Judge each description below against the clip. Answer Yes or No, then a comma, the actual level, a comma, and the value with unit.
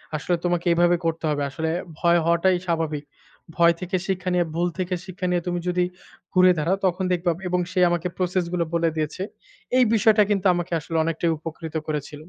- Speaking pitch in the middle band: Yes, medium, 175 Hz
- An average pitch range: No, narrow, 1.7 semitones